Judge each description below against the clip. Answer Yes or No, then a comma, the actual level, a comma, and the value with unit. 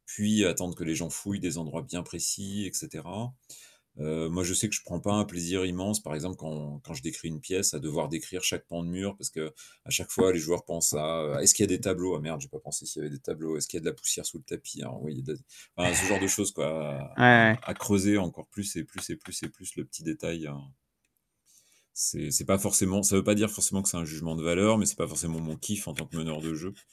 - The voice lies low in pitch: Yes, very low, 90 Hz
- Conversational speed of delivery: No, fast, 280 wpm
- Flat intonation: No, average, 3.9 semitones